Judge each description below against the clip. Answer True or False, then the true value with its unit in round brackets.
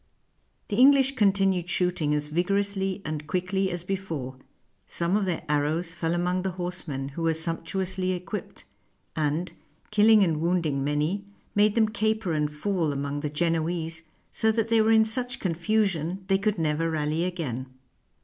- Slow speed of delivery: False (155 wpm)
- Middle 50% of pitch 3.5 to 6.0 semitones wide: True (4.0 semitones)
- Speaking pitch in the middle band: True (180 Hz)